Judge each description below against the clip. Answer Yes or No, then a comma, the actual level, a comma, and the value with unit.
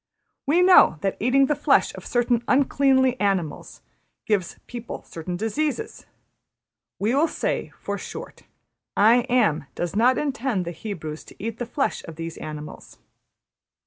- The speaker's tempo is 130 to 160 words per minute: Yes, average, 145 wpm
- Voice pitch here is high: Yes, high, 230 Hz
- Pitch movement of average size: No, wide, 6.9 semitones